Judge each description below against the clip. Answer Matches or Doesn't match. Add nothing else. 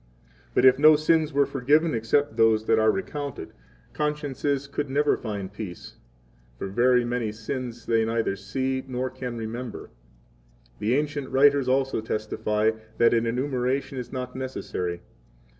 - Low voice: Matches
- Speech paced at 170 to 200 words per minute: Doesn't match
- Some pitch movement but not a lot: Matches